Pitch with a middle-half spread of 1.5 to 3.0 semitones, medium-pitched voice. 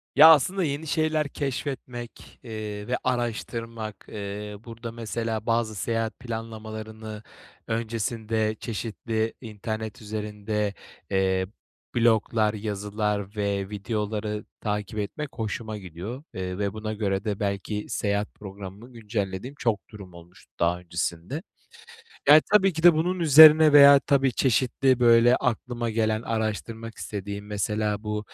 No: narrow, 2.5 semitones; low, 110 Hz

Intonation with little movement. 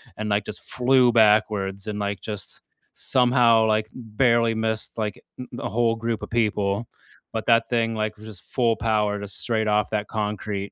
Yes: narrow, 1.8 semitones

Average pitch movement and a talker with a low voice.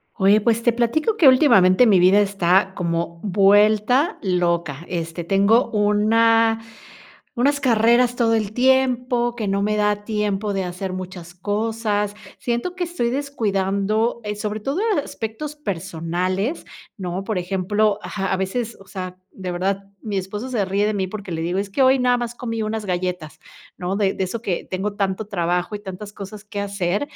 No: average, 3.4 semitones; high, 205 Hz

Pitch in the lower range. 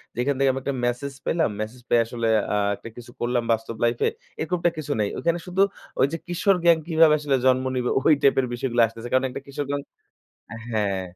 Yes: low, 130 Hz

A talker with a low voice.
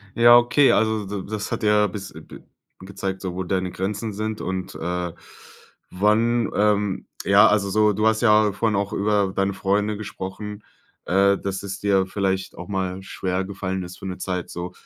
Yes: low, 100 Hz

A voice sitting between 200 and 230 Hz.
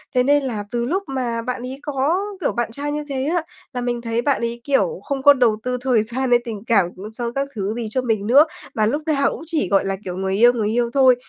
No: high, 245 Hz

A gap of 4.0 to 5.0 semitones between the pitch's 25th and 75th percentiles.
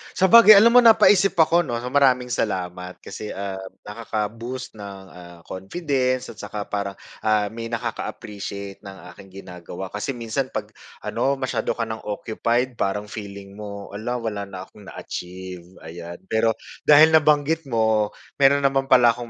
Yes: average, 4.7 semitones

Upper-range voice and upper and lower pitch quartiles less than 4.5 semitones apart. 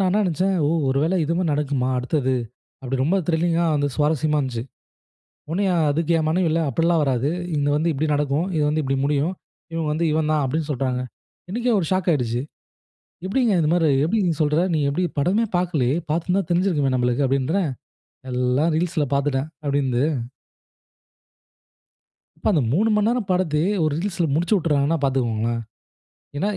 No: medium, 155 Hz; average, 4.0 semitones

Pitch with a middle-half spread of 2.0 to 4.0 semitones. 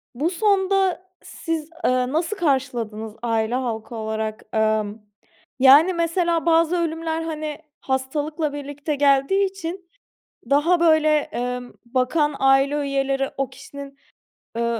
No: average, 4.6 semitones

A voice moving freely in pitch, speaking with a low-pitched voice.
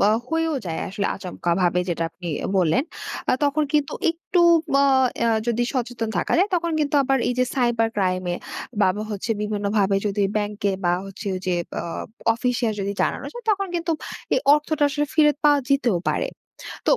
No: wide, 7.0 semitones; high, 235 Hz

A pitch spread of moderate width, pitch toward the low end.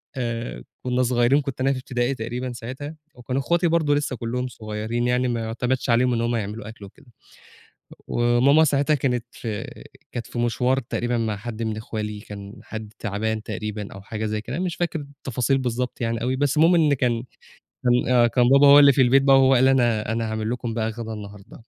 Yes: average, 3.0 semitones; low, 120 Hz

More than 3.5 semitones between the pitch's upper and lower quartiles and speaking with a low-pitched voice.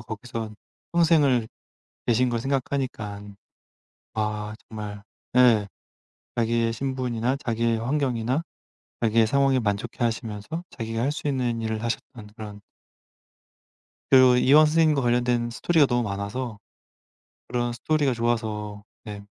No: average, 3.0 semitones; low, 120 Hz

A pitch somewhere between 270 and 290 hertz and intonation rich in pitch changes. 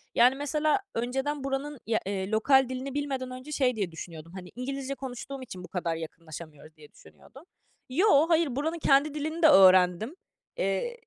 No: very high, 260 Hz; wide, 7.3 semitones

